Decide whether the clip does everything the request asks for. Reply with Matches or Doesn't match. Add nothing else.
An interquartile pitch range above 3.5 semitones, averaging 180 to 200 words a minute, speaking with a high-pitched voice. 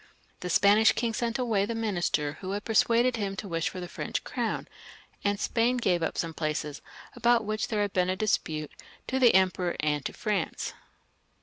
Matches